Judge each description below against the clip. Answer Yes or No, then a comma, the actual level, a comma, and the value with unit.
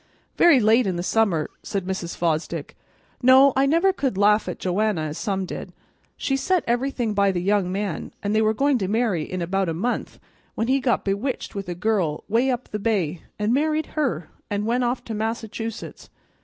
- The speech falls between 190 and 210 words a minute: Yes, average, 195 wpm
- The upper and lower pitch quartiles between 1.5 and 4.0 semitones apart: No, average, 4.7 semitones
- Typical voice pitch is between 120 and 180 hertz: No, high, 215 Hz